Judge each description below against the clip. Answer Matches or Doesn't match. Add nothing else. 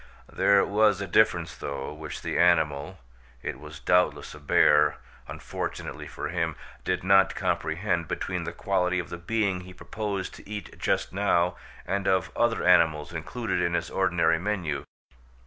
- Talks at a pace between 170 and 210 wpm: Doesn't match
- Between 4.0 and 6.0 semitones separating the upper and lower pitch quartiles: Doesn't match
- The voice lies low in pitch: Matches